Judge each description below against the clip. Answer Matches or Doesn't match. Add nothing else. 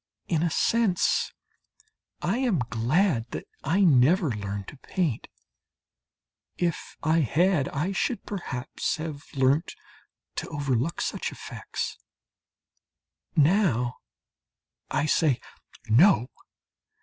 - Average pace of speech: Doesn't match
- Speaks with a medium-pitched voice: Matches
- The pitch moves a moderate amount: Doesn't match